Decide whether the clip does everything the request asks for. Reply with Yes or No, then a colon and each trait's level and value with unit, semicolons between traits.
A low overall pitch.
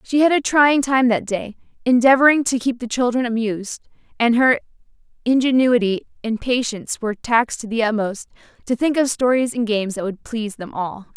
No: high, 240 Hz